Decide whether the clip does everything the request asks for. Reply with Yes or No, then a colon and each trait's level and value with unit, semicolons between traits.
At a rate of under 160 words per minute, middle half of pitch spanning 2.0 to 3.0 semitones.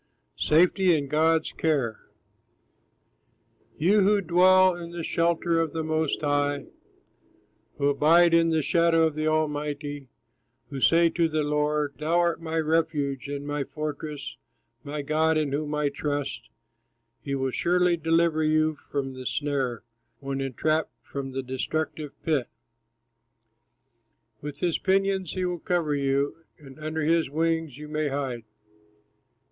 Yes: average, 140 wpm; narrow, 2.5 semitones